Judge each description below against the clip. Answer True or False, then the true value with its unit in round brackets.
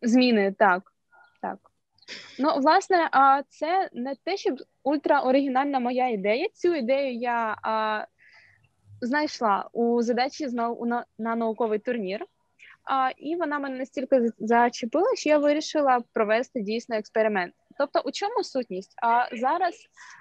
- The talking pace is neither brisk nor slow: True (115 wpm)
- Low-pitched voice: False (255 Hz)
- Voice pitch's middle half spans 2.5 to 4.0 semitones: False (4.4 semitones)